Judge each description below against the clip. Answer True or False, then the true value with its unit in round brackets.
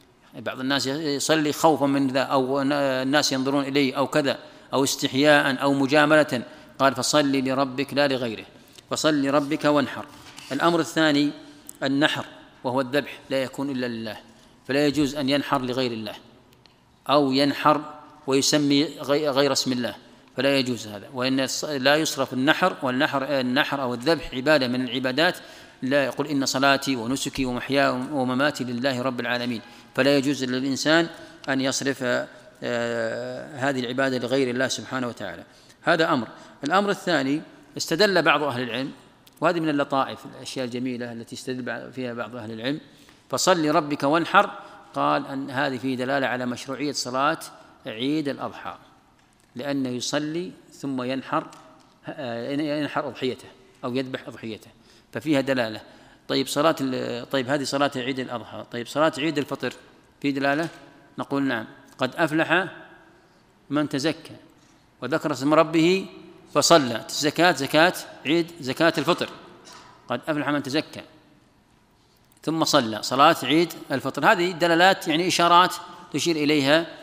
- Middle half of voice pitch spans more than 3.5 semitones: False (2.7 semitones)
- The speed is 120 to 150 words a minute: True (130 wpm)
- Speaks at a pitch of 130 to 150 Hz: True (140 Hz)